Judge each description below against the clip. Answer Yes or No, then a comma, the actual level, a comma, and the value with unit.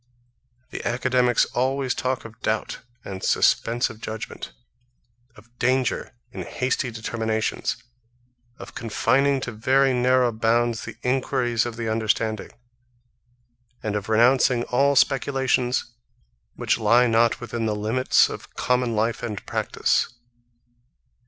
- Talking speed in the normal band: No, slow, 120 wpm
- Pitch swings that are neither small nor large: No, narrow, 2.3 semitones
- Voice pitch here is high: No, low, 120 Hz